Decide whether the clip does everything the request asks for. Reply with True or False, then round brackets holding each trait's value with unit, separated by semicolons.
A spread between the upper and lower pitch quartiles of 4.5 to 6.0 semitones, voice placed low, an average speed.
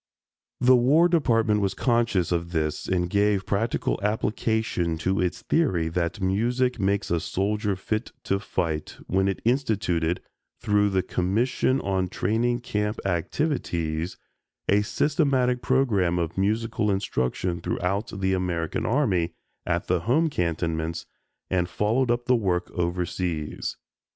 False (4.9 semitones; 100 Hz; 130 wpm)